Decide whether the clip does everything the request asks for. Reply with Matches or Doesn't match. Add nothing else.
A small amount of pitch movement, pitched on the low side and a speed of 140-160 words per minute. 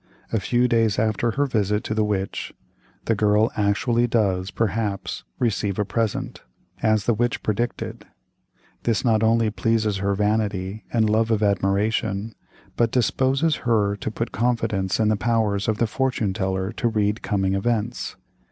Matches